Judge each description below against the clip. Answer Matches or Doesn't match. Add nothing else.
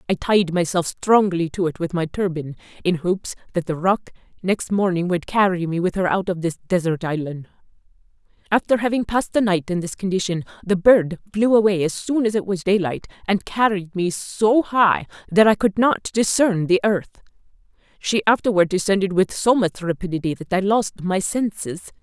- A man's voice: Doesn't match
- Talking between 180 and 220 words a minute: Matches